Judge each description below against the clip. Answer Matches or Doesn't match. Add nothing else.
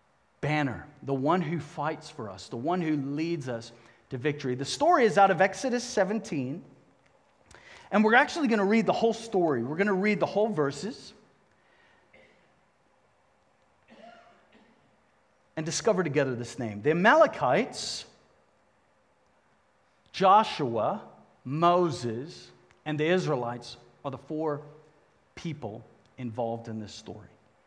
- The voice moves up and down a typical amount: Doesn't match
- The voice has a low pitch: Doesn't match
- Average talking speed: Doesn't match